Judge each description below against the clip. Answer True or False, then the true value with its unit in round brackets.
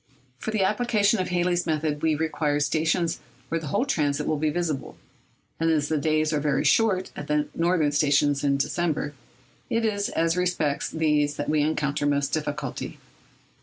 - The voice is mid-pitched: True (155 Hz)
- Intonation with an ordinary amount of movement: True (3.0 semitones)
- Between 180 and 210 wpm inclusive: False (170 wpm)